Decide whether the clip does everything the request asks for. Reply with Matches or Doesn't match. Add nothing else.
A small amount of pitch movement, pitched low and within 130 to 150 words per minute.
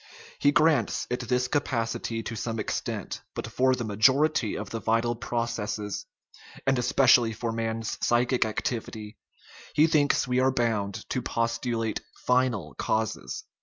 Matches